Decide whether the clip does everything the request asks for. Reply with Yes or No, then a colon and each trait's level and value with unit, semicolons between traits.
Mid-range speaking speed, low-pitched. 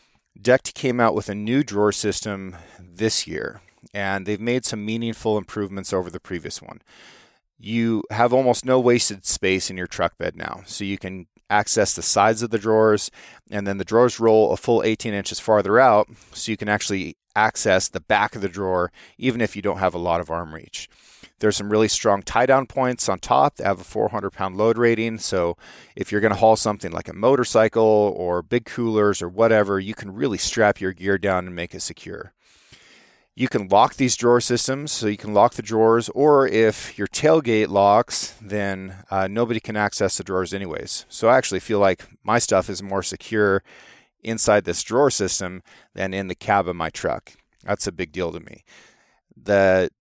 Yes: average, 195 wpm; low, 105 Hz